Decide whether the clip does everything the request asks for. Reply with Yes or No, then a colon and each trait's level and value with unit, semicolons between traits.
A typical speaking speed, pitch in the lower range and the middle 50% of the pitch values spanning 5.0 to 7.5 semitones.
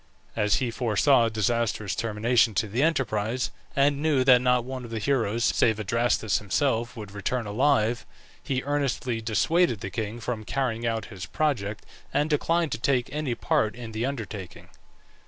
No: average, 165 wpm; low, 120 Hz; average, 3.4 semitones